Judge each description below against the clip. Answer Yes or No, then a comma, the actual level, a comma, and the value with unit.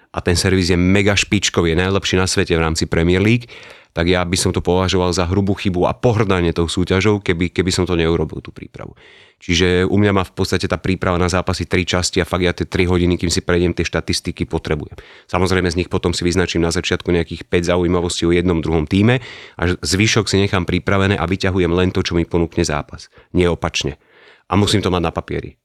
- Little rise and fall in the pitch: Yes, narrow, 1.5 semitones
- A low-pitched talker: Yes, very low, 90 Hz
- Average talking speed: No, fast, 220 wpm